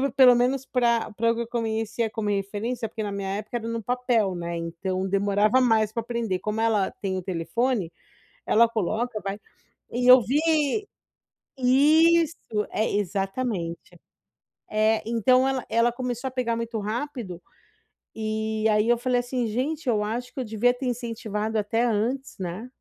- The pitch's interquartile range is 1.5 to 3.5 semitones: Yes, average, 3.0 semitones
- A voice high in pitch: Yes, high, 230 Hz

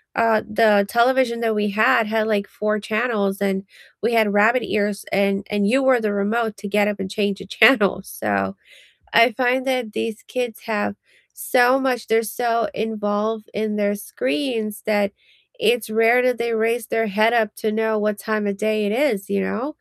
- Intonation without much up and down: Yes, narrow, 2.2 semitones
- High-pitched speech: Yes, high, 215 Hz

